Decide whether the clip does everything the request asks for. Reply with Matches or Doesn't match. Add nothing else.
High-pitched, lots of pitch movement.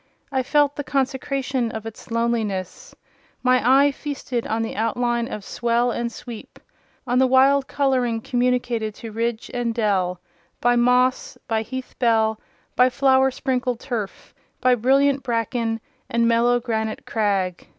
Doesn't match